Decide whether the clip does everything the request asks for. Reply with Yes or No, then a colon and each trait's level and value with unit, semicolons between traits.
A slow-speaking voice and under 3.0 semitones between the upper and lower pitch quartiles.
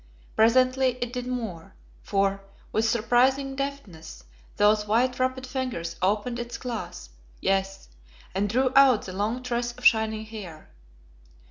No: slow, 130 wpm; average, 4.0 semitones